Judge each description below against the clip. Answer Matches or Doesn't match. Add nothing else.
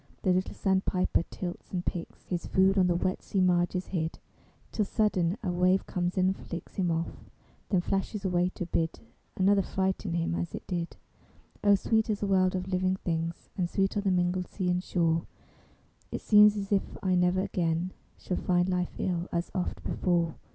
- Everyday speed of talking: Matches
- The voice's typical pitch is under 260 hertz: Matches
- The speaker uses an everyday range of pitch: Doesn't match